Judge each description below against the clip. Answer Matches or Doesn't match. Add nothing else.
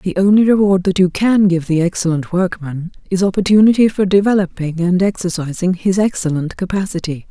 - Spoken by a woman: Matches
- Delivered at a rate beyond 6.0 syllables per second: Doesn't match